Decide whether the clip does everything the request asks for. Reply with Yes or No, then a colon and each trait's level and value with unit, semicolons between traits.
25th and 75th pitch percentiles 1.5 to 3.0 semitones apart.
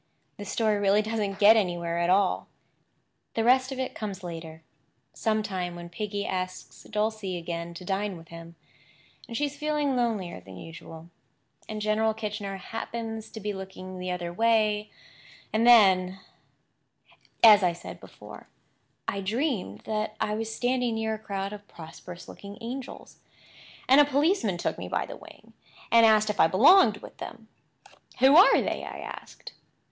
No: average, 3.6 semitones